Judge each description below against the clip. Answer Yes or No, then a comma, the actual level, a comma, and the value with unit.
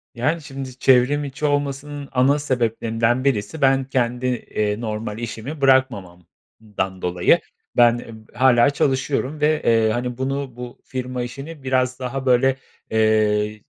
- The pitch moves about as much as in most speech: Yes, average, 3.2 semitones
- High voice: No, low, 125 Hz